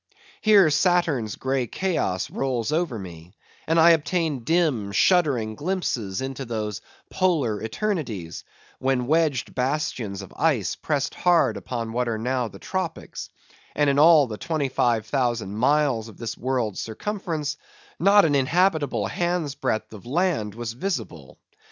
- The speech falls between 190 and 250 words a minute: No, slow, 135 wpm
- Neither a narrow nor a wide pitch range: No, wide, 6.4 semitones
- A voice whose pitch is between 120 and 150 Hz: Yes, low, 135 Hz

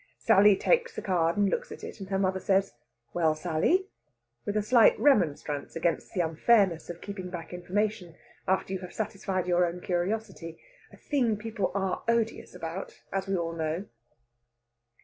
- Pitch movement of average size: Yes, average, 3.5 semitones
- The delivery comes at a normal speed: Yes, average, 170 wpm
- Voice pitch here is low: No, high, 190 Hz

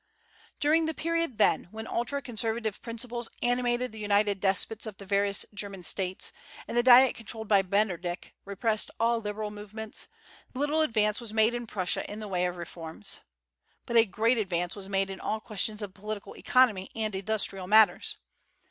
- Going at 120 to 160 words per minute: No, average, 170 wpm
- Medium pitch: No, high, 215 Hz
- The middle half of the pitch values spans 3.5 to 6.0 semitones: No, average, 3.0 semitones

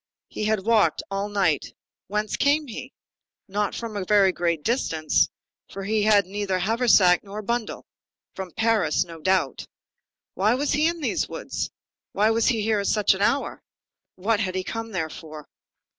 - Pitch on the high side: Yes, high, 205 Hz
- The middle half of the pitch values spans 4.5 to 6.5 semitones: No, average, 3.2 semitones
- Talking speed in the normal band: Yes, average, 170 wpm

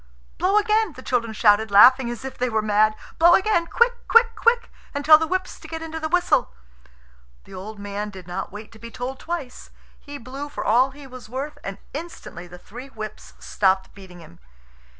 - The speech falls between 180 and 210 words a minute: Yes, average, 200 wpm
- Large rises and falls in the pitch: Yes, wide, 7.3 semitones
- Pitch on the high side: Yes, very high, 255 Hz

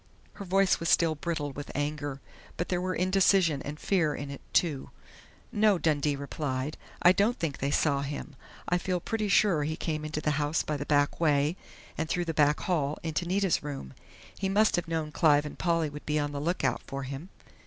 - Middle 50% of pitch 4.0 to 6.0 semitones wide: No, average, 3.4 semitones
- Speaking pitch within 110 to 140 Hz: No, medium, 155 Hz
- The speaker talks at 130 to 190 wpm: No, fast, 205 wpm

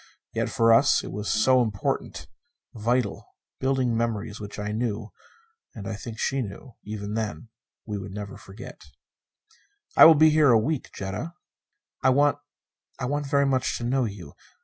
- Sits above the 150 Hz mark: No, low, 115 Hz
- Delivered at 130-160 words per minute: No, average, 170 wpm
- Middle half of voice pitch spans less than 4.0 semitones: No, average, 4.3 semitones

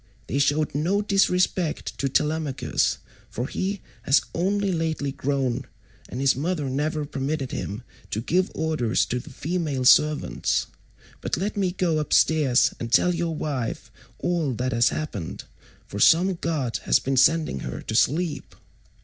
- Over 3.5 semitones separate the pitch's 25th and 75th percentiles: Yes, average, 4.4 semitones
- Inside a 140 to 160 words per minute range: Yes, average, 150 wpm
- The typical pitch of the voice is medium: Yes, medium, 150 Hz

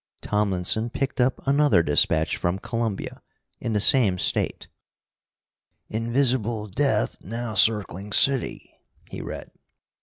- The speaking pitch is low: Yes, low, 110 Hz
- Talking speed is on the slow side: Yes, slow, 110 wpm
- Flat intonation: No, average, 4.2 semitones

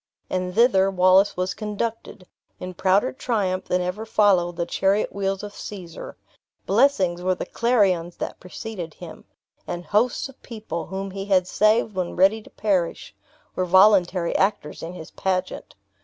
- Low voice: No, high, 190 Hz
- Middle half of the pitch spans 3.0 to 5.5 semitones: No, narrow, 2.6 semitones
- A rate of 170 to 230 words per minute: No, average, 155 wpm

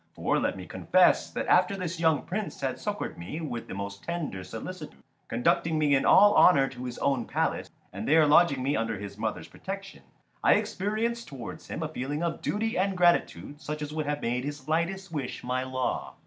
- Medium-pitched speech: Yes, medium, 150 Hz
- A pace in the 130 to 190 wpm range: No, average, 200 wpm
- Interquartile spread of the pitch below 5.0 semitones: No, wide, 5.5 semitones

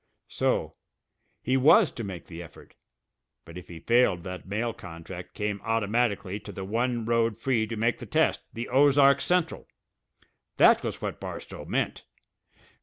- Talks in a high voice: No, low, 115 Hz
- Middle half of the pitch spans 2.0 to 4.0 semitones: No, average, 4.4 semitones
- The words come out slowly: No, average, 155 wpm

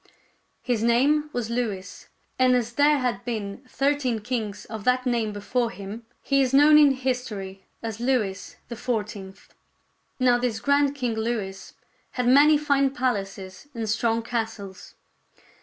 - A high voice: Yes, high, 235 Hz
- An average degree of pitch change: Yes, average, 3.4 semitones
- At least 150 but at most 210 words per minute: No, average, 140 wpm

